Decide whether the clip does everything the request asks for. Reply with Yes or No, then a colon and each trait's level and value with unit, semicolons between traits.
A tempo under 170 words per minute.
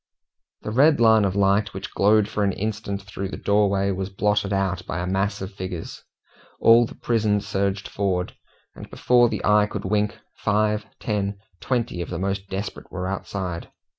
No: average, 175 wpm